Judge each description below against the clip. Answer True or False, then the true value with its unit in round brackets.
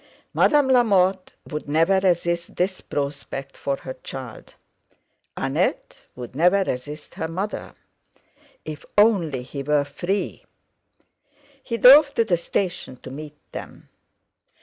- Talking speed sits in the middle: False (120 wpm)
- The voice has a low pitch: False (170 Hz)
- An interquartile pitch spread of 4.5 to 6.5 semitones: True (5.4 semitones)